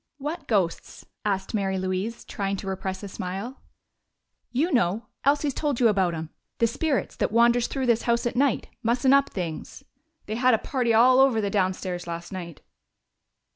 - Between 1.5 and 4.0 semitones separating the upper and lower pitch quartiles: No, average, 5.1 semitones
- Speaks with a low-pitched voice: No, high, 220 Hz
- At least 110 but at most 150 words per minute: No, average, 175 wpm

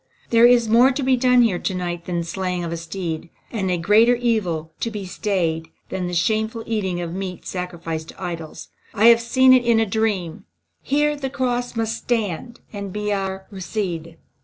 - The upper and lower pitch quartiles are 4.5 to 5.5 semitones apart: Yes, average, 5.0 semitones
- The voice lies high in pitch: Yes, high, 200 Hz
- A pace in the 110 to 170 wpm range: No, average, 195 wpm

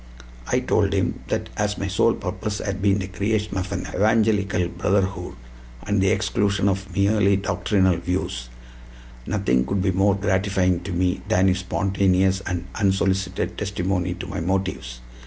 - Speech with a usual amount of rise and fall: No, narrow, 1.4 semitones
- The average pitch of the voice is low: Yes, very low, 95 Hz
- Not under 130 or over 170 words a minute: Yes, average, 155 wpm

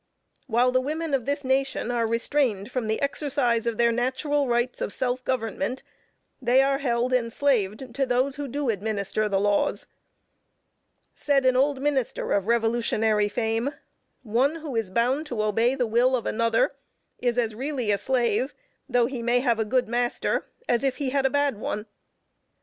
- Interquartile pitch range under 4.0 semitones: Yes, average, 3.0 semitones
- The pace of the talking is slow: No, average, 170 wpm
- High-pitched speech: Yes, high, 245 Hz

